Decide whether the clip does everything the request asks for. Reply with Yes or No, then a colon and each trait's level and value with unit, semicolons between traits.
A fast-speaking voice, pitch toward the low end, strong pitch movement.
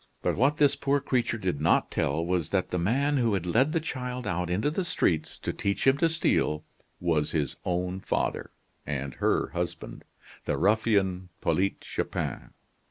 No: average, 170 wpm; low, 100 Hz; wide, 7.3 semitones